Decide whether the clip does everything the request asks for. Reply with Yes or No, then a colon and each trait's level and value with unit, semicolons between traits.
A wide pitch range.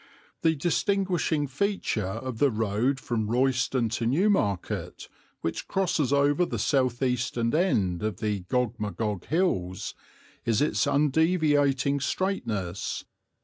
Yes: wide, 6.0 semitones